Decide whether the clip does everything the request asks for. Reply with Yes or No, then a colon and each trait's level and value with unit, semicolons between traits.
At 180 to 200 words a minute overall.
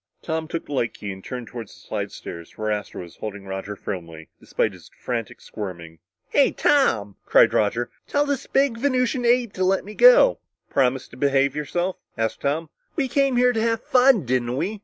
Yes: average, 185 wpm